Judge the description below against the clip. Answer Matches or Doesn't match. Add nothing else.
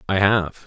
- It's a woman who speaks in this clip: Doesn't match